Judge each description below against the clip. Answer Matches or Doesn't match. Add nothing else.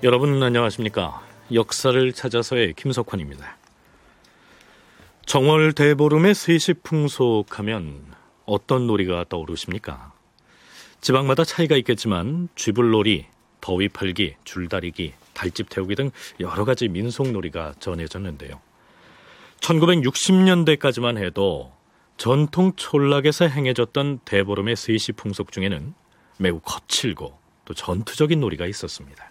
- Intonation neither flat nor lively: Doesn't match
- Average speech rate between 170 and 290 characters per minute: Matches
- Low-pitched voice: Matches